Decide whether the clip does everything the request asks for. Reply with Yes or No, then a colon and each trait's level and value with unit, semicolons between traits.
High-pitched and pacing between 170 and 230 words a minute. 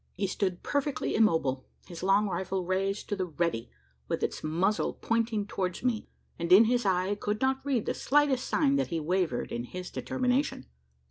Yes: high, 195 Hz; average, 185 wpm